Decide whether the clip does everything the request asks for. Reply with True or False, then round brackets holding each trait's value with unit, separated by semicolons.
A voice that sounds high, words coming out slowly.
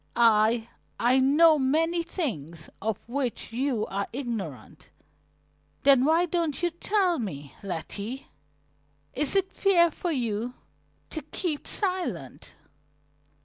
True (265 Hz; 110 wpm)